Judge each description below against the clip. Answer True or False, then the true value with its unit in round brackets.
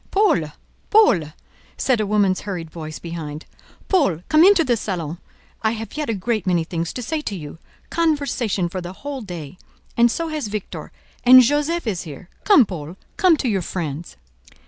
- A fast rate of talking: False (170 wpm)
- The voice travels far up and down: True (8.8 semitones)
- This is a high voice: True (205 Hz)